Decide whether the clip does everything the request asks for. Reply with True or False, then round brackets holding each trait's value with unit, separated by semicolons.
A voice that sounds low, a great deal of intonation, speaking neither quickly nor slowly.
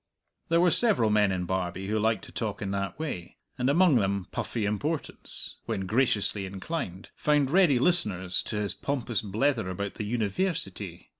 True (105 Hz; 6.8 semitones; 165 wpm)